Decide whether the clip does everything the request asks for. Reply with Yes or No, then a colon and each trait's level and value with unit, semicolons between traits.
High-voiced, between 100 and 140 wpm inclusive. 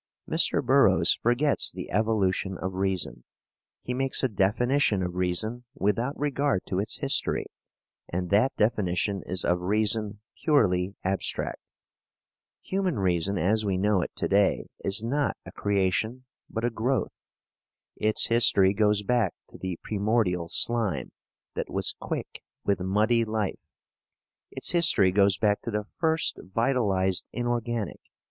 No: low, 105 Hz; slow, 135 wpm